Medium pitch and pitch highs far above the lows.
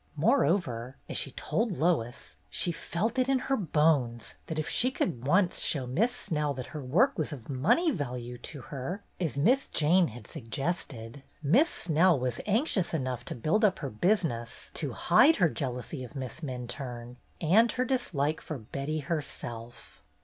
Yes: medium, 150 Hz; wide, 6.6 semitones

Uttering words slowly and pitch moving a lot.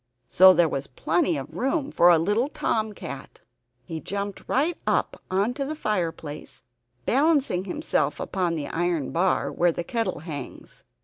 No: average, 150 wpm; wide, 5.7 semitones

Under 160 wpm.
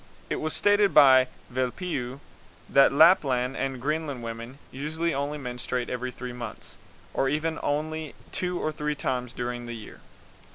Yes: average, 150 wpm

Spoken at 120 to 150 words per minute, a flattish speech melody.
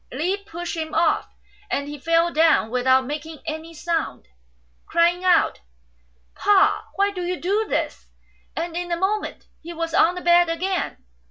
No: average, 165 wpm; narrow, 2.1 semitones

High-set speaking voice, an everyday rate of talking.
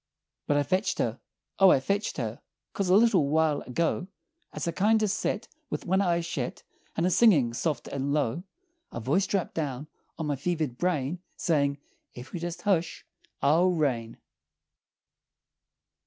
No: medium, 160 Hz; average, 155 wpm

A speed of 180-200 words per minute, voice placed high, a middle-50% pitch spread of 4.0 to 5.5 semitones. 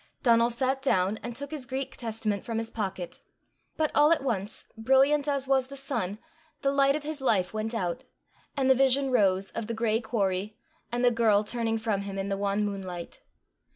Yes: average, 195 wpm; high, 230 Hz; average, 4.8 semitones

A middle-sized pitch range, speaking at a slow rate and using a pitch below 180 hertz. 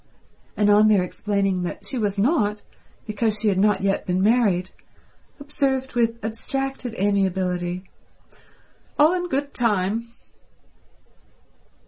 No: average, 4.1 semitones; slow, 115 wpm; high, 210 Hz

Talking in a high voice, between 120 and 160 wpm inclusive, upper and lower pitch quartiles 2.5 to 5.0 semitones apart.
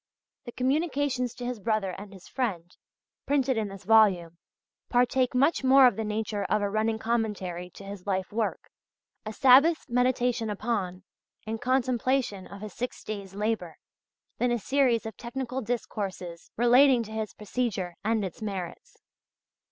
Yes: high, 225 Hz; average, 150 wpm; average, 3.9 semitones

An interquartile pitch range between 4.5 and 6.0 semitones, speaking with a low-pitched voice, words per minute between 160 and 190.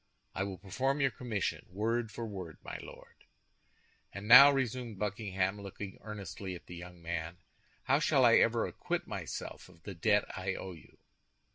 No: average, 3.6 semitones; low, 100 Hz; average, 165 wpm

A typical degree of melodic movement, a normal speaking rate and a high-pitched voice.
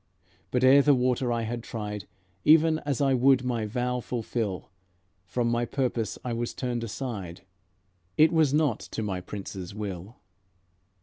No: average, 3.6 semitones; average, 150 wpm; low, 120 Hz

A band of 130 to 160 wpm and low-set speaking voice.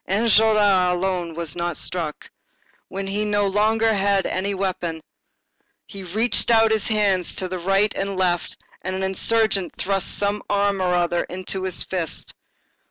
No: average, 150 wpm; high, 195 Hz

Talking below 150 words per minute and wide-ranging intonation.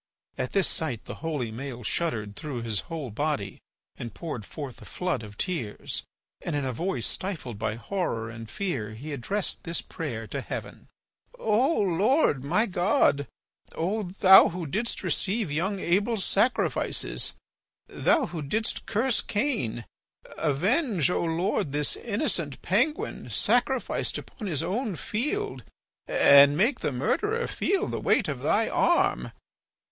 Yes: average, 140 wpm; wide, 7.7 semitones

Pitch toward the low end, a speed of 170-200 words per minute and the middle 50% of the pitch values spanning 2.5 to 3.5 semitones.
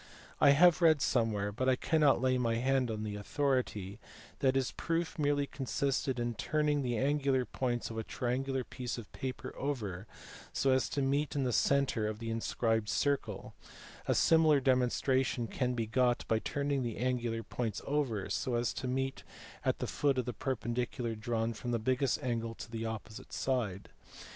Yes: low, 125 Hz; average, 180 wpm; average, 3.1 semitones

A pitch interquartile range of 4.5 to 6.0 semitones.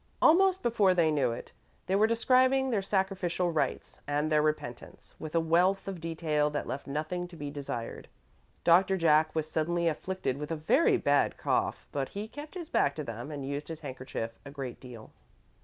Yes: average, 4.8 semitones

